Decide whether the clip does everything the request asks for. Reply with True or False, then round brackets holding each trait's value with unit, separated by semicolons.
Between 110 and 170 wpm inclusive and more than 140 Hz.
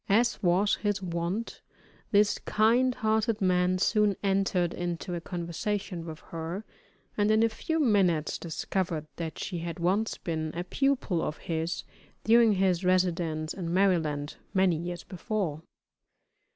True (140 wpm; 185 Hz)